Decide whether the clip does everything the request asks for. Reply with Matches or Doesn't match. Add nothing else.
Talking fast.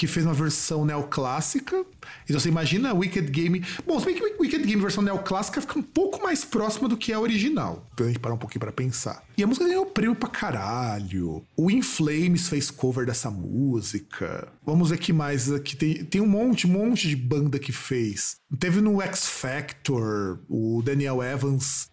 Matches